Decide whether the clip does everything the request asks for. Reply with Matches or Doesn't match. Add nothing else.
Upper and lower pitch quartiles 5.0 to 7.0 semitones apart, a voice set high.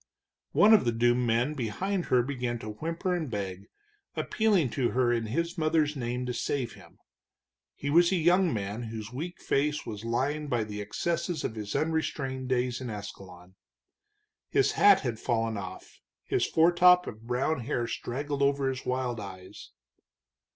Doesn't match